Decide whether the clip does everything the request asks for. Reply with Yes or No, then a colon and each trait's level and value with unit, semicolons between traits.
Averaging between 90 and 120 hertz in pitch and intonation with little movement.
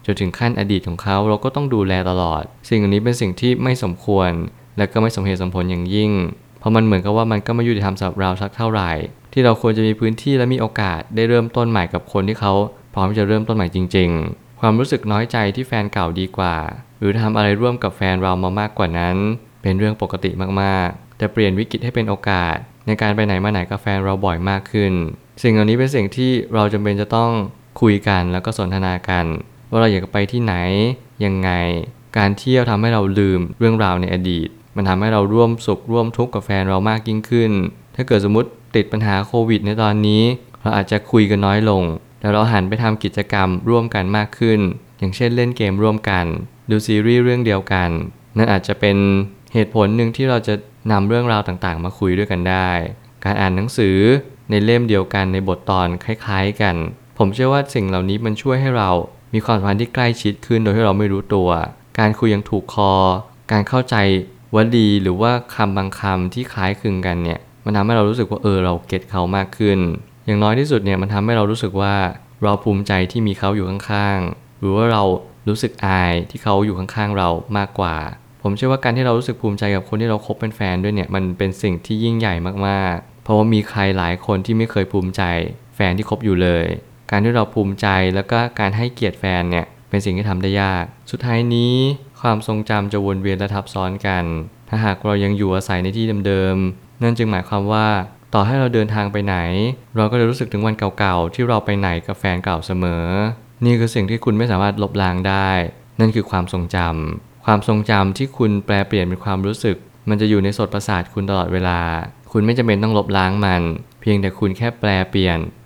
No: low, 105 Hz; average, 3.1 semitones